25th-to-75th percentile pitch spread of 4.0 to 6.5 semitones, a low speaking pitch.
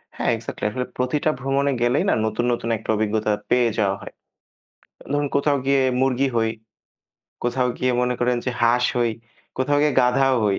No: narrow, 2.6 semitones; low, 125 Hz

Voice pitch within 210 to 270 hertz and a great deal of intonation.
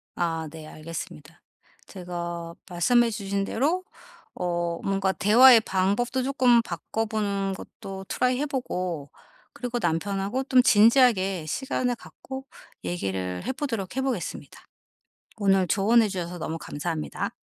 No: high, 195 Hz; wide, 5.8 semitones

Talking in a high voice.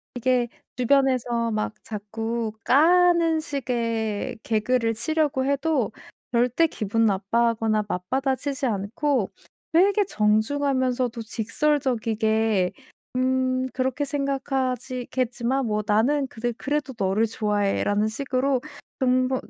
Yes: very high, 250 Hz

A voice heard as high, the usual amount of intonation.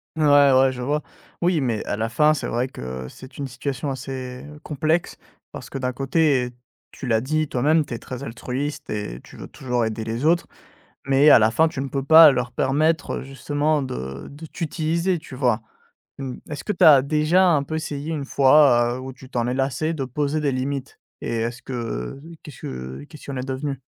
No: low, 135 Hz; average, 3.5 semitones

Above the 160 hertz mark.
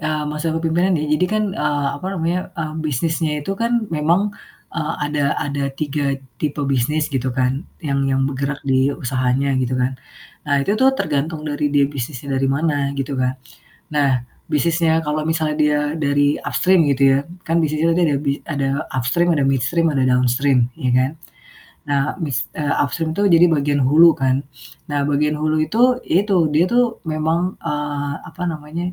No: medium, 150 Hz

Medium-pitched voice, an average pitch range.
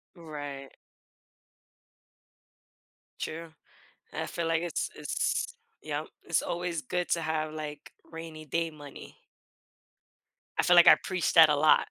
No: medium, 160 Hz; narrow, 1.8 semitones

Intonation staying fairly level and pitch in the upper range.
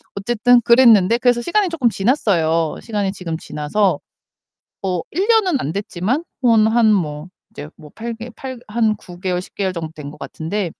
No: wide, 5.4 semitones; high, 210 Hz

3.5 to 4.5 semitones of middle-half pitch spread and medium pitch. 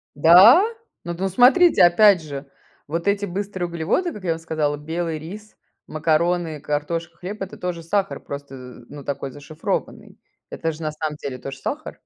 Yes: average, 4.2 semitones; medium, 165 Hz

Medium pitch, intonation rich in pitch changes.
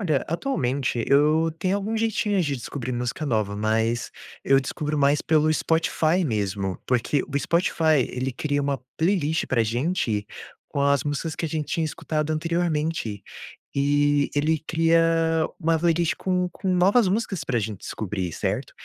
No: medium, 150 Hz; average, 4.7 semitones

